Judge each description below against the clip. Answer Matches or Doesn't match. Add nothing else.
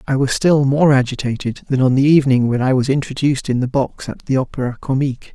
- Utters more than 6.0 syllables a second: Matches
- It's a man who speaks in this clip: Matches